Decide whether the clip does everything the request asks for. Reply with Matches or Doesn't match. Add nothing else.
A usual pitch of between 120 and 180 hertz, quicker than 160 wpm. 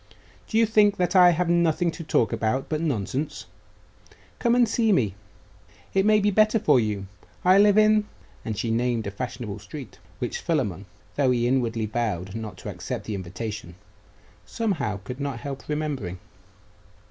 Matches